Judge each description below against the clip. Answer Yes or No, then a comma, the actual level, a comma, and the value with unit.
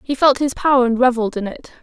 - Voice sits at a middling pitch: No, very high, 250 Hz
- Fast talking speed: Yes, fast, 265 wpm